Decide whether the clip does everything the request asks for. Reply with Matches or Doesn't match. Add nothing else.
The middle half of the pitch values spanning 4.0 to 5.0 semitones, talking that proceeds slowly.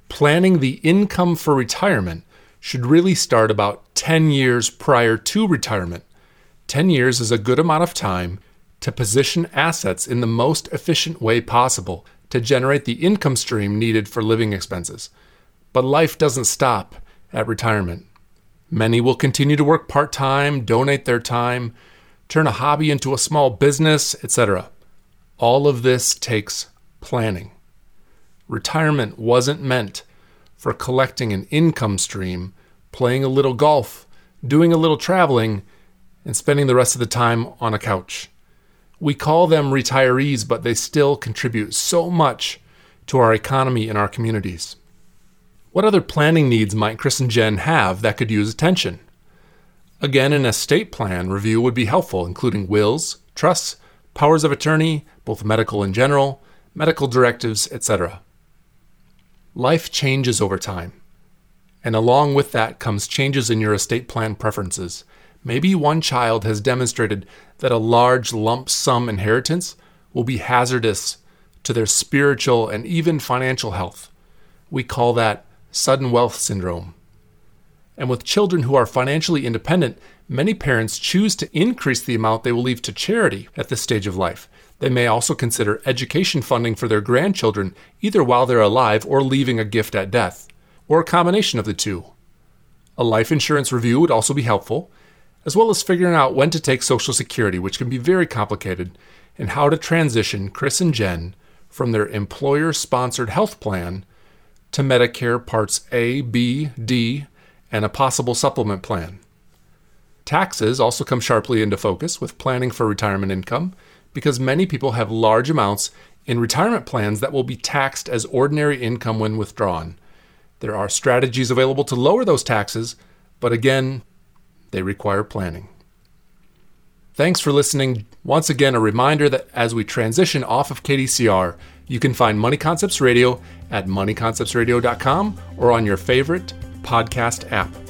Doesn't match